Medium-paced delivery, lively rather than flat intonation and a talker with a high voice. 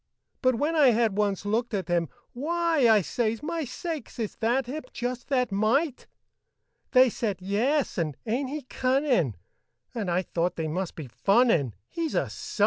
Yes: average, 170 wpm; wide, 5.7 semitones; high, 235 Hz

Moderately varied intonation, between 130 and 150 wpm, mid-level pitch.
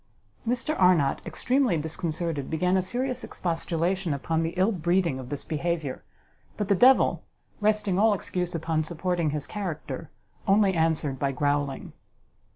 Yes: average, 4.0 semitones; average, 140 wpm; medium, 170 Hz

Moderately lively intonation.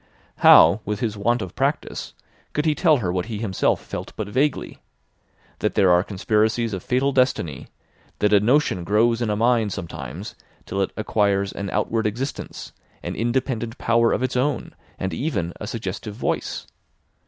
Yes: average, 3.6 semitones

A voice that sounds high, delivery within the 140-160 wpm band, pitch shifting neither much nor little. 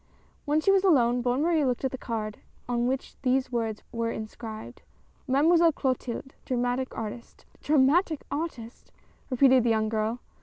Yes: very high, 255 Hz; average, 150 wpm; average, 3.5 semitones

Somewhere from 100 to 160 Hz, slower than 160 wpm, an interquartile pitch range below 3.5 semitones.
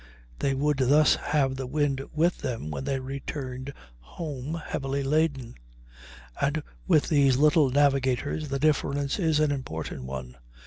Yes: medium, 140 Hz; average, 140 wpm; narrow, 2.4 semitones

